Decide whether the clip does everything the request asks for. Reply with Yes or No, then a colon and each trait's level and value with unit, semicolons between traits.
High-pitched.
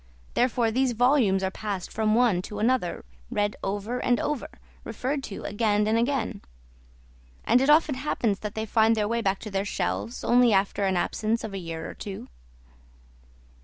Yes: high, 220 Hz